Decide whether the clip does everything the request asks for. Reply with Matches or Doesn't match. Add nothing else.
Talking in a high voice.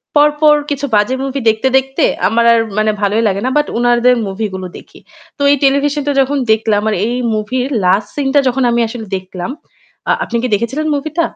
Matches